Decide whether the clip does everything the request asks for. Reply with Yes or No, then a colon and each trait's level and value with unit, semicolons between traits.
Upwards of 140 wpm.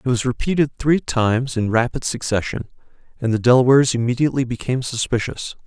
Yes: average, 150 wpm